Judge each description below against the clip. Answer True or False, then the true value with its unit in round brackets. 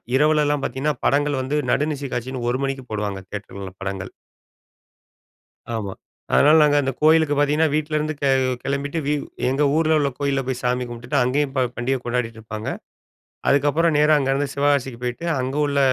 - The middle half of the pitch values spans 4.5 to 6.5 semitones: False (3.1 semitones)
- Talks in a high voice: False (140 Hz)